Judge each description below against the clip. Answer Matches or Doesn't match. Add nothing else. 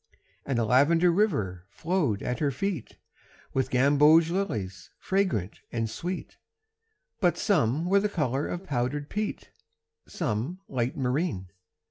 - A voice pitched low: Doesn't match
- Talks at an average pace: Doesn't match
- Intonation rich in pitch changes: Matches